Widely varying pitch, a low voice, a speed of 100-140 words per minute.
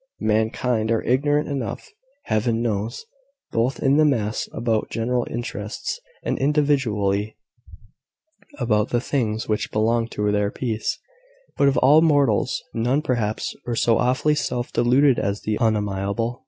No: average, 3.7 semitones; low, 115 Hz; slow, 135 wpm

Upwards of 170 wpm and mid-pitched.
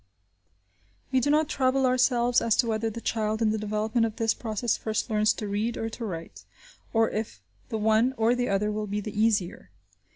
No: average, 200 wpm; high, 220 Hz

